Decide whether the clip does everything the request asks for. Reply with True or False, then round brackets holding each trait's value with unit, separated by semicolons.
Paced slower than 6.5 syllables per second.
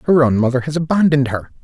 False (7.2 syllables/s)